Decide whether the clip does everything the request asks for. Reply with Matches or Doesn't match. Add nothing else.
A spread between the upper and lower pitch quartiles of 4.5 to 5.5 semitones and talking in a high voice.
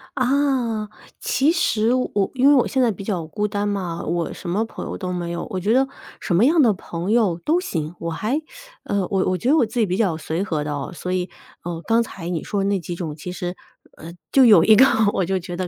Matches